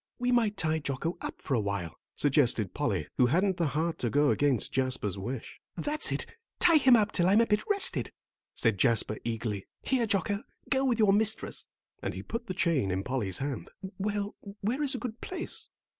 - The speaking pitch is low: No, medium, 170 Hz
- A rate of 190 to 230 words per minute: Yes, average, 195 wpm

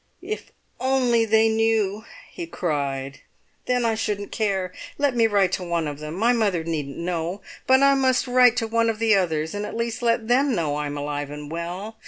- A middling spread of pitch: No, wide, 6.0 semitones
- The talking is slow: No, fast, 205 wpm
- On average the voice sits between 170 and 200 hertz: No, high, 210 Hz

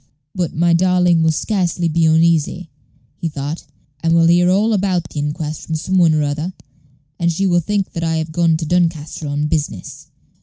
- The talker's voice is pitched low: No, medium, 165 Hz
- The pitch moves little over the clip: Yes, narrow, 2.2 semitones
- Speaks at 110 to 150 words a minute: No, average, 190 wpm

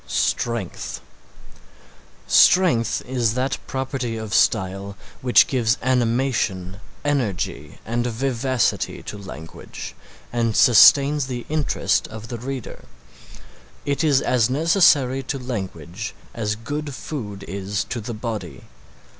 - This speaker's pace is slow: Yes, slow, 110 wpm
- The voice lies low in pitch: Yes, low, 120 Hz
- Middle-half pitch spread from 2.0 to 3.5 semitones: No, average, 4.1 semitones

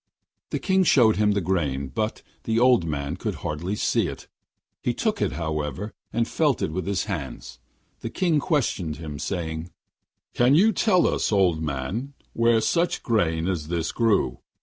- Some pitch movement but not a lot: No, wide, 6.8 semitones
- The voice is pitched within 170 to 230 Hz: No, very low, 95 Hz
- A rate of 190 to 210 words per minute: No, average, 170 wpm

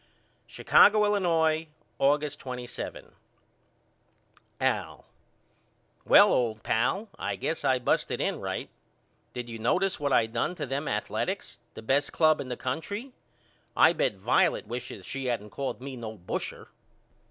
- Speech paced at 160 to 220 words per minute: No, average, 140 wpm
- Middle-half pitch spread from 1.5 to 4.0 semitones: No, average, 5.0 semitones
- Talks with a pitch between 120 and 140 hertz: Yes, low, 135 Hz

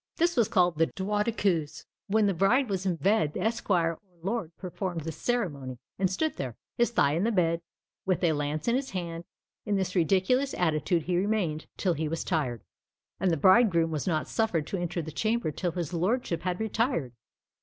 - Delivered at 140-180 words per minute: No, average, 200 wpm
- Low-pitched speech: No, medium, 180 Hz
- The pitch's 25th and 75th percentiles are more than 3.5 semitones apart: Yes, average, 4.4 semitones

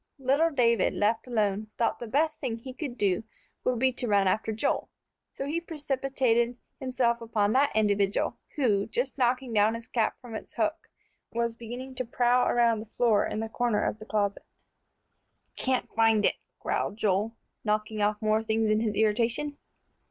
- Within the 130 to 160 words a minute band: No, average, 175 wpm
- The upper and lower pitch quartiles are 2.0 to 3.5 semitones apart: Yes, average, 2.8 semitones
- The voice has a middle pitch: No, high, 230 Hz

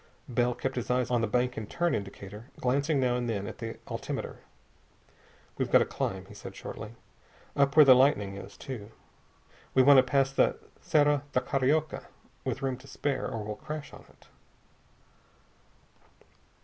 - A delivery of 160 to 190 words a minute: Yes, average, 170 wpm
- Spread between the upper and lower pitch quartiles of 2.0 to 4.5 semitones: Yes, average, 3.6 semitones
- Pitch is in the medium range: No, low, 125 Hz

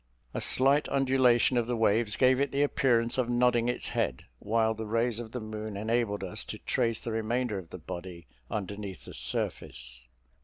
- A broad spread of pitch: No, average, 2.8 semitones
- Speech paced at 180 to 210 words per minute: Yes, average, 185 wpm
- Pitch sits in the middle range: No, low, 115 Hz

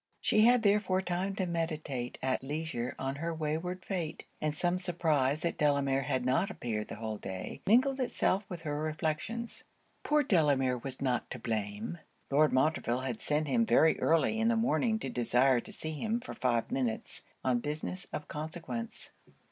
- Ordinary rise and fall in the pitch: No, wide, 6.0 semitones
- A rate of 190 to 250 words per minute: No, average, 170 wpm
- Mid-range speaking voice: Yes, medium, 155 Hz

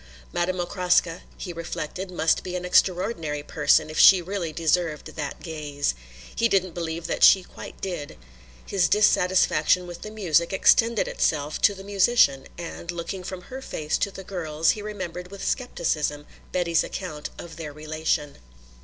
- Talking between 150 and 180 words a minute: Yes, average, 155 wpm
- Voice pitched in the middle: Yes, medium, 175 Hz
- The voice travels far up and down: No, average, 3.2 semitones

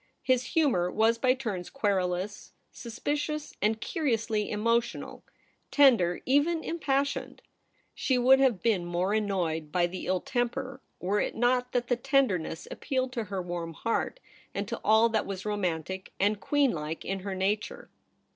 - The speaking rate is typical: Yes, average, 160 wpm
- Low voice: No, high, 220 Hz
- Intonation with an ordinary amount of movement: No, wide, 5.7 semitones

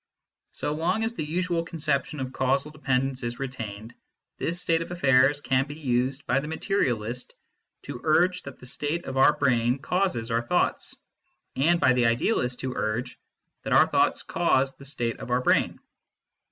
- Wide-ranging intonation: No, average, 4.2 semitones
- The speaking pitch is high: No, low, 135 Hz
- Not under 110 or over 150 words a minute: No, average, 175 wpm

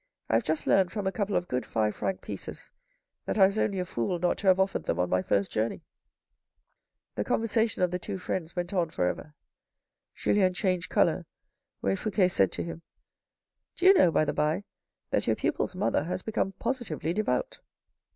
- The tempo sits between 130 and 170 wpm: No, average, 200 wpm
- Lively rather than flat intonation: No, average, 4.5 semitones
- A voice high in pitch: No, medium, 180 Hz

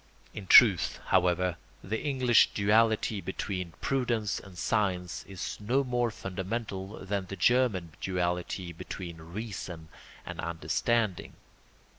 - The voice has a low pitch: Yes, very low, 95 Hz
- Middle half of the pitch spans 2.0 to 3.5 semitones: No, average, 4.0 semitones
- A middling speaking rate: No, slow, 110 wpm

